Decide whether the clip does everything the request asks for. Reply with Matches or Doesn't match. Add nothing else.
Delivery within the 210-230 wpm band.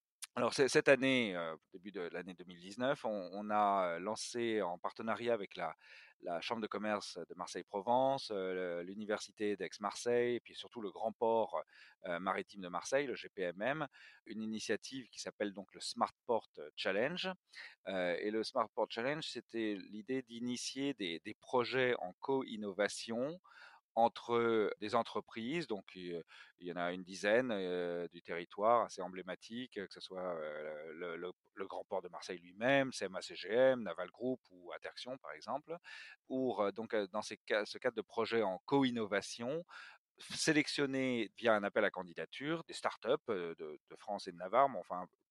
Doesn't match